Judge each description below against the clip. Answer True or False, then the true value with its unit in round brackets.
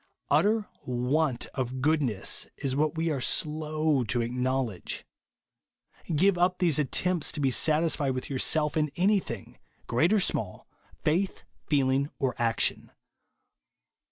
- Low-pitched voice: False (145 Hz)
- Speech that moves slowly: True (125 wpm)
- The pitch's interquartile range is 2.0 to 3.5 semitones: False (4.0 semitones)